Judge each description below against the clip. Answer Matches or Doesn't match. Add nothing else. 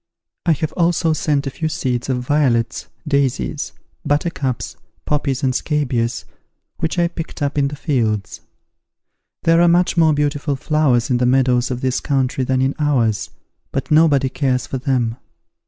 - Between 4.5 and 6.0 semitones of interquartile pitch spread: Doesn't match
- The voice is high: Doesn't match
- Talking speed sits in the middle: Matches